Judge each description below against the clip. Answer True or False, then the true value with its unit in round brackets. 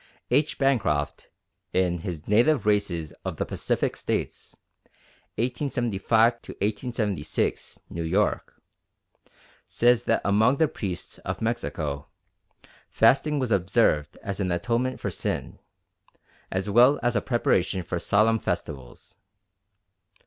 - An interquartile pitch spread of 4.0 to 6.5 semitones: True (5.2 semitones)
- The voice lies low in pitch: True (105 Hz)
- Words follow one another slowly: True (110 wpm)